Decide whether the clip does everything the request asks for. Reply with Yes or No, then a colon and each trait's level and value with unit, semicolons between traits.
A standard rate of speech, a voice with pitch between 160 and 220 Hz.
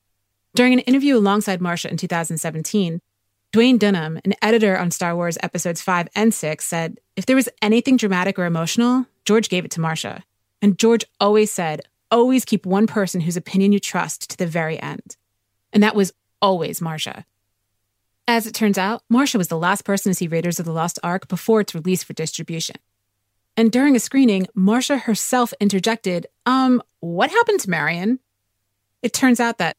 Yes: average, 180 wpm; high, 190 Hz